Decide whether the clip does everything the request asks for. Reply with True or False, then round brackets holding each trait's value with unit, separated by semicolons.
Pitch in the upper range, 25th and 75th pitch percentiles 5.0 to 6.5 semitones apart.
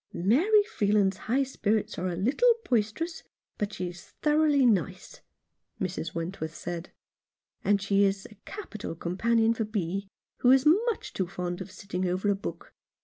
True (200 Hz; 5.6 semitones)